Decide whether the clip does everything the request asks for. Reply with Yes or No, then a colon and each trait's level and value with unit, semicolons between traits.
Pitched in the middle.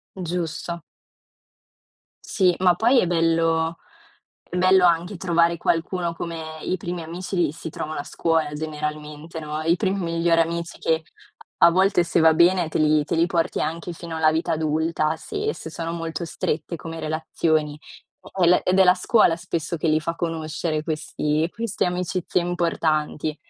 Yes: medium, 165 Hz